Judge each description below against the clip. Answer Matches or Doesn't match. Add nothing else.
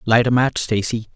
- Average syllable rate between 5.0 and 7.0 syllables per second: Matches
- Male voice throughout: Matches